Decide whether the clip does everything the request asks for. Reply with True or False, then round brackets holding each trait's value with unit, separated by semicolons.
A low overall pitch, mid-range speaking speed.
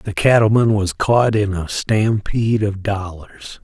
True (105 Hz; 150 wpm)